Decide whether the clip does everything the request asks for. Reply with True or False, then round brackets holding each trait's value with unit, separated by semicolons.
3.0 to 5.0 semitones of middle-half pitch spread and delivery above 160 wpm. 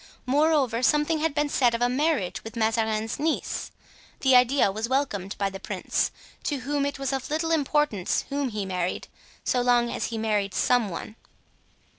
True (4.7 semitones; 175 wpm)